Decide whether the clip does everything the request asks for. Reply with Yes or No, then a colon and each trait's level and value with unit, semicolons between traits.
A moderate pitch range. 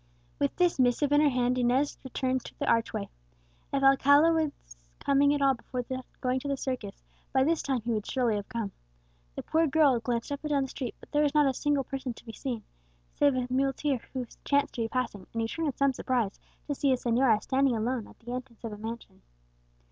Yes: average, 3.1 semitones